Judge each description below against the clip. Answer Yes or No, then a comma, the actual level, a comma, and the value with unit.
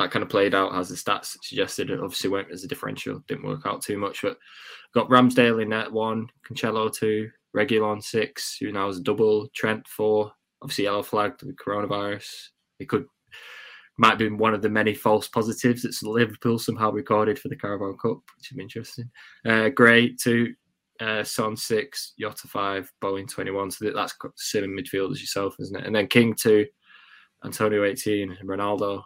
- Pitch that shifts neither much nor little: No, narrow, 2.3 semitones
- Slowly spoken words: No, average, 190 wpm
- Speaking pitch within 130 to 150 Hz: No, low, 110 Hz